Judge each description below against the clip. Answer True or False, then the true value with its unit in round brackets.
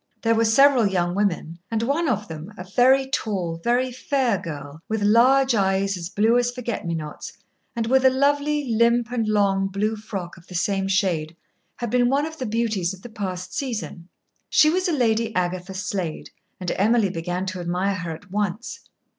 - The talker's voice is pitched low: False (210 Hz)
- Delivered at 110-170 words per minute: False (190 wpm)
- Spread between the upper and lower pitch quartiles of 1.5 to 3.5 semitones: False (4.9 semitones)